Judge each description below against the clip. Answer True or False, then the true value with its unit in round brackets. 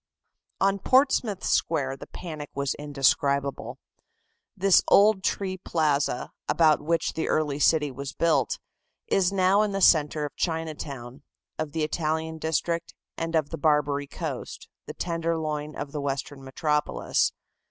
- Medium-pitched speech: True (155 Hz)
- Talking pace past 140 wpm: False (135 wpm)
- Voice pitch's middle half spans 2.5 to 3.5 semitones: True (2.8 semitones)